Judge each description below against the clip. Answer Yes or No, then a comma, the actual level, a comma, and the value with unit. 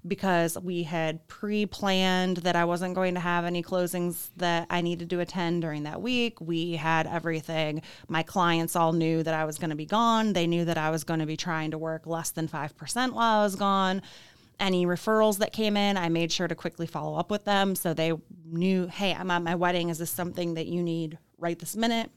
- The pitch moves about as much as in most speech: No, narrow, 2.2 semitones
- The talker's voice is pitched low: No, medium, 175 Hz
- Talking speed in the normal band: No, fast, 225 wpm